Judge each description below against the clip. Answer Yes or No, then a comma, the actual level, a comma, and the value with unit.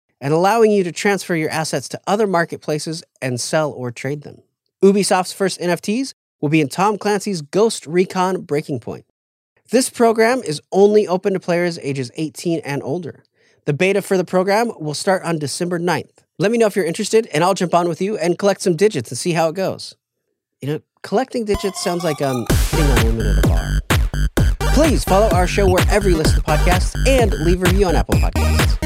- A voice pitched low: No, medium, 175 Hz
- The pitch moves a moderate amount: Yes, average, 5.0 semitones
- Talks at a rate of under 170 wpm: No, fast, 205 wpm